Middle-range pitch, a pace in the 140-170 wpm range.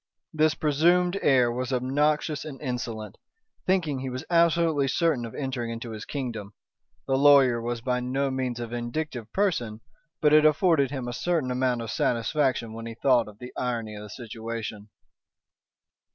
No: low, 130 Hz; average, 165 wpm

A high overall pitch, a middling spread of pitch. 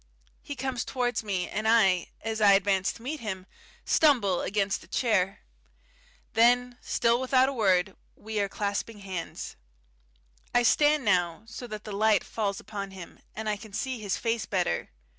Yes: high, 215 Hz; average, 3.6 semitones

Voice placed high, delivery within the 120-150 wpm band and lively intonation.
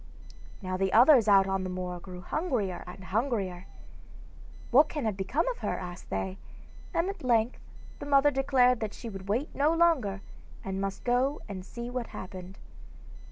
No: high, 220 Hz; average, 175 wpm; wide, 6.0 semitones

